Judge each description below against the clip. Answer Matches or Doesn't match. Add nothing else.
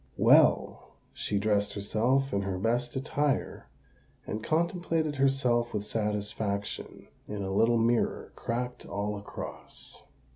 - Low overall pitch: Matches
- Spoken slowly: Matches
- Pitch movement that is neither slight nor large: Matches